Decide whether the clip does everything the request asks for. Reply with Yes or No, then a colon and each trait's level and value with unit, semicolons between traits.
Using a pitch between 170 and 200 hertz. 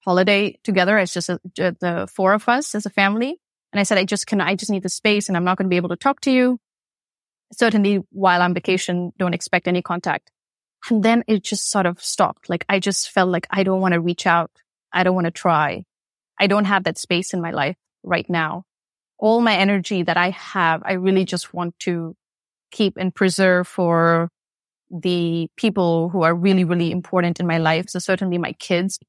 Yes: medium, 185 Hz